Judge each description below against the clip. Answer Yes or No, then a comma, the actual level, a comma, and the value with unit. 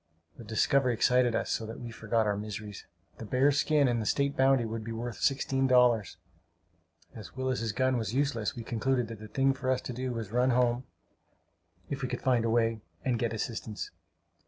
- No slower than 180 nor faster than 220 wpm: Yes, fast, 205 wpm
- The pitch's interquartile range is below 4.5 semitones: Yes, narrow, 2.6 semitones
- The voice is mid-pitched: No, low, 120 Hz